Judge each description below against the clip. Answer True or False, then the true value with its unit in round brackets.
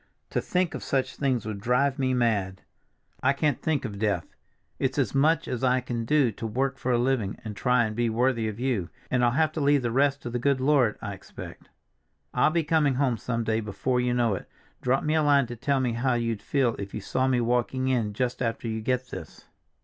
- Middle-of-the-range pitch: False (125 Hz)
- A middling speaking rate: False (230 wpm)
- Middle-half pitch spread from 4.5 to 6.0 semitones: False (3.1 semitones)